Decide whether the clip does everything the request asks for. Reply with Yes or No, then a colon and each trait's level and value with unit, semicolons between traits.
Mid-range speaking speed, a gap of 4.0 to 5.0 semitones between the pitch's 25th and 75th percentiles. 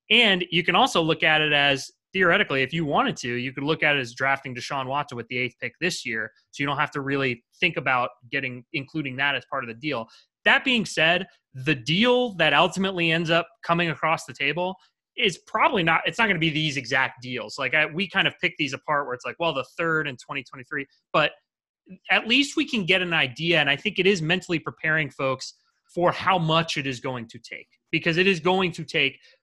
No: fast, 230 wpm; average, 4.6 semitones